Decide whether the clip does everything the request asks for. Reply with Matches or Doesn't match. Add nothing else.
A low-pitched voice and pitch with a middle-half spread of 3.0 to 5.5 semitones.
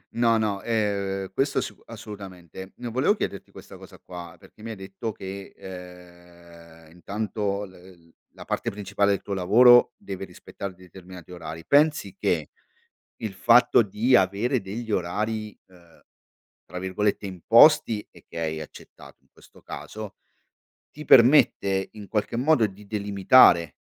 Matches